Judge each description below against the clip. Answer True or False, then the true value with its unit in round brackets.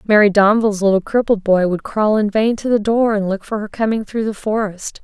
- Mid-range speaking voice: False (210 Hz)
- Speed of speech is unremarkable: False (240 wpm)